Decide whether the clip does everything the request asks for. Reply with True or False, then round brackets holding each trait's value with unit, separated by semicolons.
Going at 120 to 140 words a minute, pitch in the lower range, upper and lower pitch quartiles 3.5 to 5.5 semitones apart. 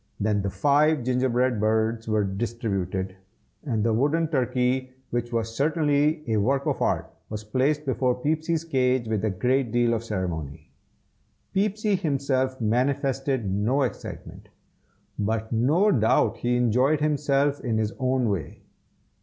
True (135 wpm; 125 Hz; 4.2 semitones)